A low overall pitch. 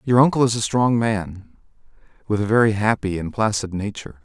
Yes: low, 105 Hz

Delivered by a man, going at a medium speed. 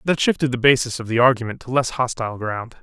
No: male; fast, 235 wpm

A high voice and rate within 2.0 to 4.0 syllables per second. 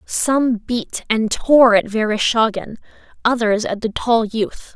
Yes: high, 225 Hz; 3.7 syllables/s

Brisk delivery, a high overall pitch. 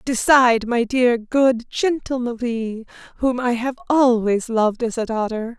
No: average, 150 wpm; high, 240 Hz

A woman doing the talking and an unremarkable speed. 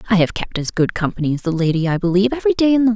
No: female; fast, 325 wpm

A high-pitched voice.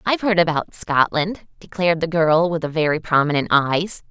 No: medium, 165 Hz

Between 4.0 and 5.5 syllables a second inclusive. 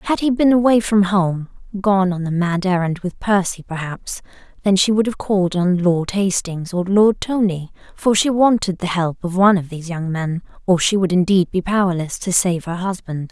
Yes: 5.0 syllables/s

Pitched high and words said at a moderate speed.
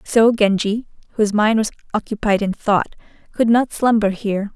Yes: high, 215 Hz; average, 160 wpm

